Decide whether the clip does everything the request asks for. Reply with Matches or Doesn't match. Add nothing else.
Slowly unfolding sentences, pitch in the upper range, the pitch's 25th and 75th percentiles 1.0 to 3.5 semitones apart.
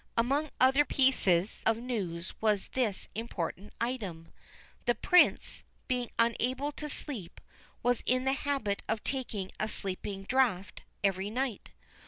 Doesn't match